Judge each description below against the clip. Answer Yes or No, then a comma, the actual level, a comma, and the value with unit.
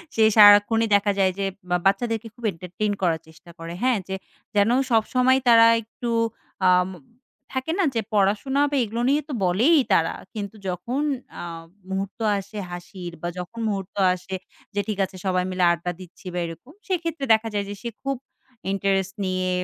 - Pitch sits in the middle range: No, high, 205 Hz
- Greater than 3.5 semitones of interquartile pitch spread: Yes, average, 4.0 semitones